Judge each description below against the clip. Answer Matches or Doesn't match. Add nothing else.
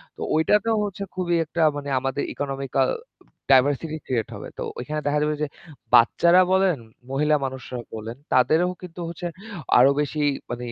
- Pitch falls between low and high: Matches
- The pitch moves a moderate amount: Matches